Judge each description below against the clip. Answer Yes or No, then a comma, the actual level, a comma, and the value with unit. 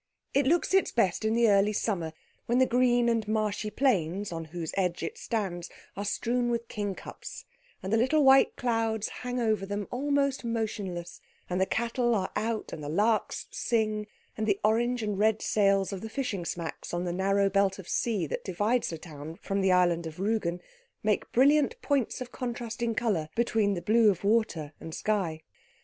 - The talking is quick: No, average, 185 wpm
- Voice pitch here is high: Yes, high, 215 Hz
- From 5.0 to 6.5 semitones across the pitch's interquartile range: No, average, 3.9 semitones